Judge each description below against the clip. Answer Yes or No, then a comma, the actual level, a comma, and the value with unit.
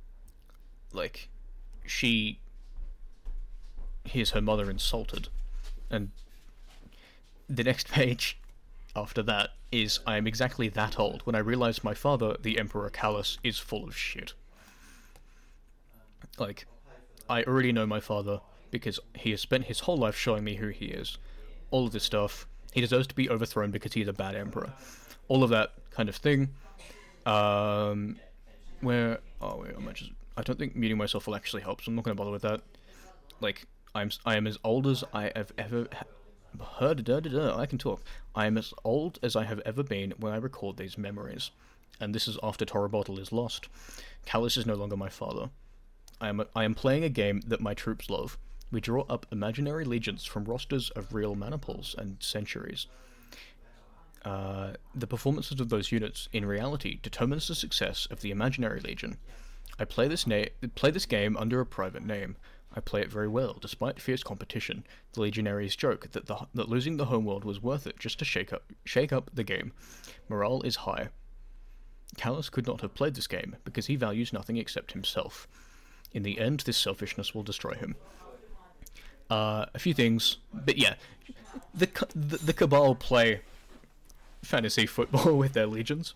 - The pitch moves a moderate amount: Yes, average, 3.4 semitones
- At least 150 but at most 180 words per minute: Yes, average, 175 wpm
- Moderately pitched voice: No, low, 110 Hz